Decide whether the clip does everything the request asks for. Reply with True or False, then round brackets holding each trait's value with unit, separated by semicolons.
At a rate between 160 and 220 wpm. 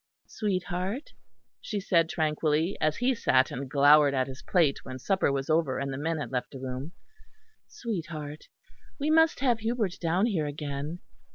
True (165 wpm)